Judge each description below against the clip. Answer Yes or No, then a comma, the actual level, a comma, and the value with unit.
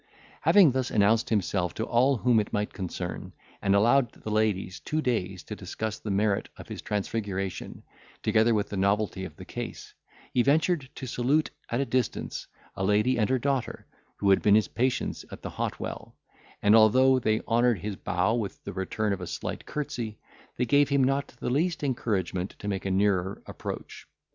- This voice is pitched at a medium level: No, low, 110 Hz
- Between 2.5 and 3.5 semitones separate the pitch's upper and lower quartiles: No, average, 4.3 semitones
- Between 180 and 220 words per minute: Yes, average, 185 wpm